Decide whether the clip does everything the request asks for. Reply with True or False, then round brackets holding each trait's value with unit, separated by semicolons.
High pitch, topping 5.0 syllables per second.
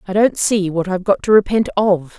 True (195 Hz; 5.6 syllables/s)